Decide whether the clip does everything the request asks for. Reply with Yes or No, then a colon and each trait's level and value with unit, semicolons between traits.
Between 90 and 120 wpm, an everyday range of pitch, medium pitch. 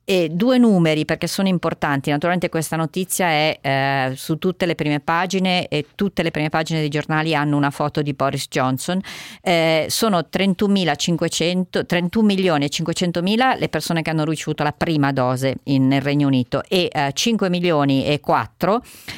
No: average, 160 wpm; average, 3.7 semitones; medium, 160 Hz